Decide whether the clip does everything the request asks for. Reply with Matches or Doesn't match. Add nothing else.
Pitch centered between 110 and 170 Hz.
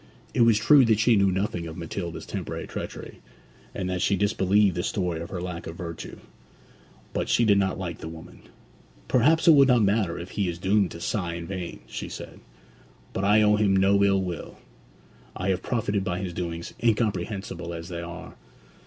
Doesn't match